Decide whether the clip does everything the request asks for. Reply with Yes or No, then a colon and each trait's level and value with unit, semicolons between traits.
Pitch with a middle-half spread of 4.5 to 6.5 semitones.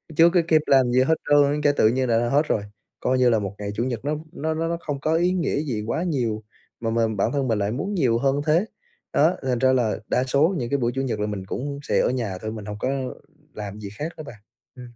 Yes: average, 4.8 semitones